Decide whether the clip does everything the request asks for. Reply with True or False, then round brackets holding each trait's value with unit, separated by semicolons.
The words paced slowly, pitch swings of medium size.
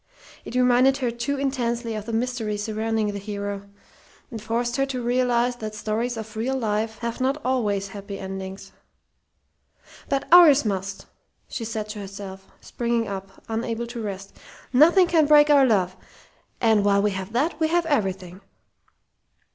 False (155 wpm; 3.8 semitones)